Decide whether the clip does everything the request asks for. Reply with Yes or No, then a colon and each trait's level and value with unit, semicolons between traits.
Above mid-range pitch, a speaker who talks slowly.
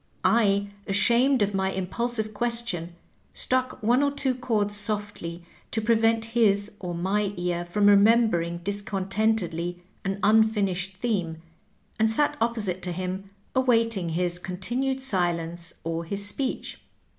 Yes: high, 205 Hz; slow, 130 wpm